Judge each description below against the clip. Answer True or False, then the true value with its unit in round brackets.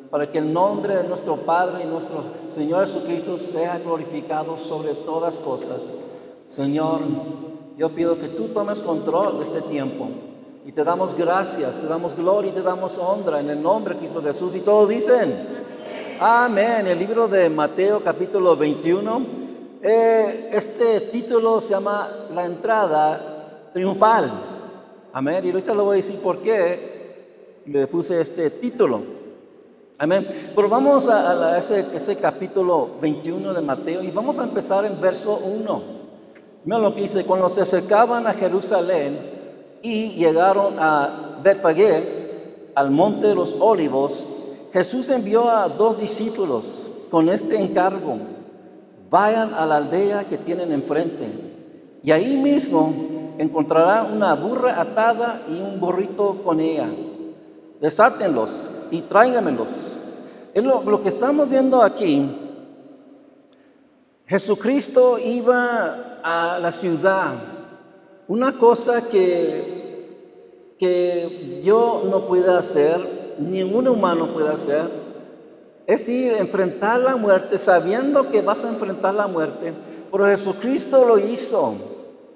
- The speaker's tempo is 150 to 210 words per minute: False (130 wpm)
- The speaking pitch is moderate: False (195 Hz)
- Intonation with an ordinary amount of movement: False (5.8 semitones)